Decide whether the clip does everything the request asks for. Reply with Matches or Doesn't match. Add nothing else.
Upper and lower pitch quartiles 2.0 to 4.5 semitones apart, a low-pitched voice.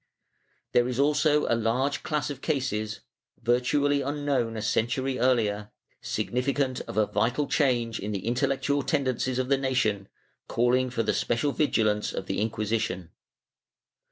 Matches